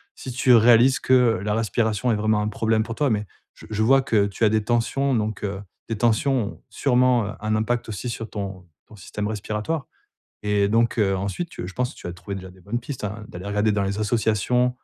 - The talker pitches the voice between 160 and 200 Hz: No, low, 110 Hz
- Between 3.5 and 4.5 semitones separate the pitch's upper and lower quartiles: No, average, 2.8 semitones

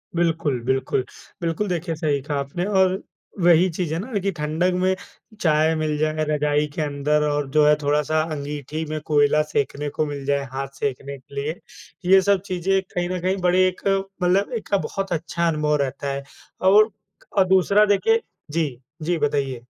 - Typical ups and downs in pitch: Yes, average, 4.0 semitones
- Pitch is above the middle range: No, medium, 155 Hz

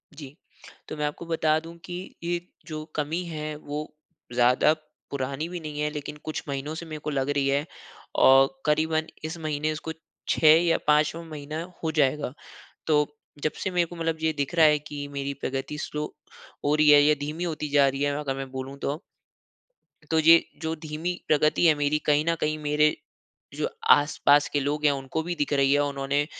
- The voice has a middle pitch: Yes, medium, 150 Hz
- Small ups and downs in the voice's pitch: Yes, narrow, 1.8 semitones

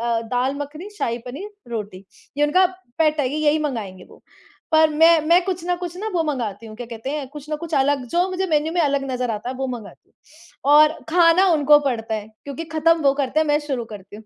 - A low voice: No, very high, 290 Hz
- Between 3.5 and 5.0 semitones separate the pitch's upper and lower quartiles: Yes, average, 4.7 semitones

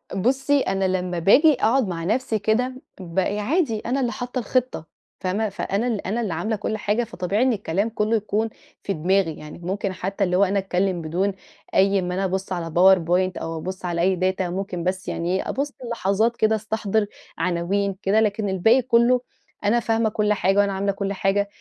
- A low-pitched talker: No, high, 200 Hz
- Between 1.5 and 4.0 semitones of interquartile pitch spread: Yes, average, 3.1 semitones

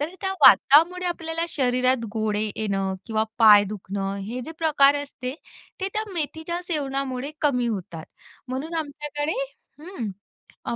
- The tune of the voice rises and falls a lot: Yes, wide, 6.5 semitones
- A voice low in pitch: No, very high, 275 Hz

